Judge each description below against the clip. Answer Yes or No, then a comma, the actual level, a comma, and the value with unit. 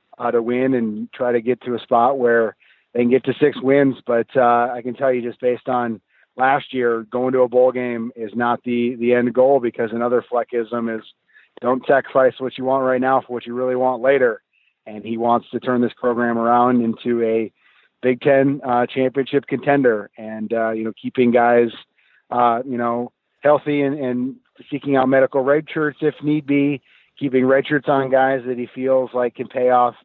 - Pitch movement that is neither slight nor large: No, narrow, 1.8 semitones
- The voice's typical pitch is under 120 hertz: No, low, 125 Hz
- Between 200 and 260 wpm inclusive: Yes, fast, 205 wpm